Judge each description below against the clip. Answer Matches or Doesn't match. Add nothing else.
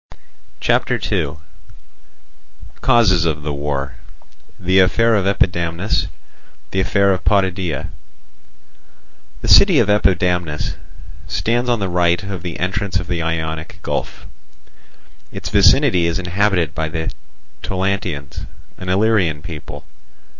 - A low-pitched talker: Matches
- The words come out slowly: Matches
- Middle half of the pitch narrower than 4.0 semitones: Matches